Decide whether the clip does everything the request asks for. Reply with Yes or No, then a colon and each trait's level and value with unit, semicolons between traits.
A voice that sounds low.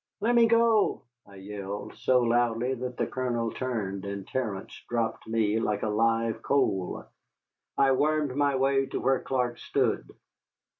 Yes: low, 120 Hz